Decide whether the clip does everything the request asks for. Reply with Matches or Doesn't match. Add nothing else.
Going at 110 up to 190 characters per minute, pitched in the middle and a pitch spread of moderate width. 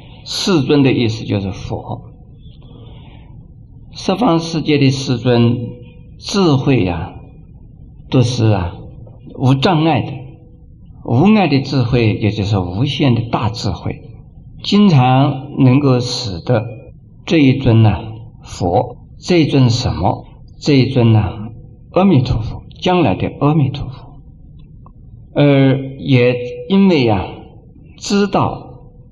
Doesn't match